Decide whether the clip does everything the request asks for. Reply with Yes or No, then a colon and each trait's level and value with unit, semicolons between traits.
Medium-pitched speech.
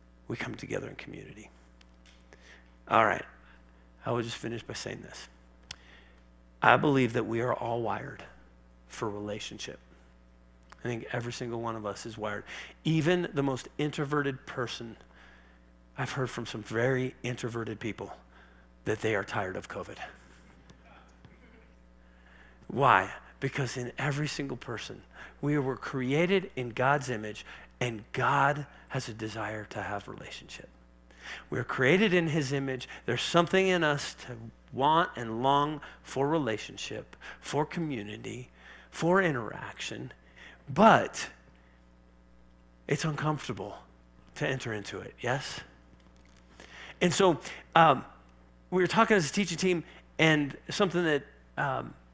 No: low, 115 Hz